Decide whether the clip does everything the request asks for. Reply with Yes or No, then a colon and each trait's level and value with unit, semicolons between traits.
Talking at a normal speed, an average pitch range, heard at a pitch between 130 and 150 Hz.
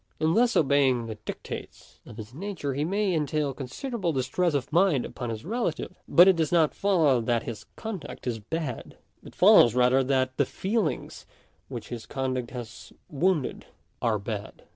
No: average, 165 wpm; wide, 5.8 semitones; medium, 140 Hz